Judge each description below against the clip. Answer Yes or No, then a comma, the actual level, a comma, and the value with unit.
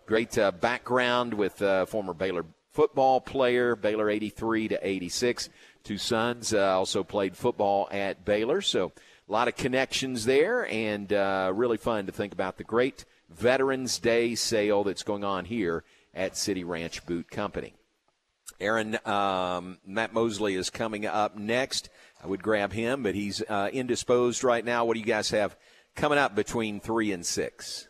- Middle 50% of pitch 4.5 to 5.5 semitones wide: No, average, 3.2 semitones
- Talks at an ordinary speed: Yes, average, 170 wpm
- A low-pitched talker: Yes, low, 105 Hz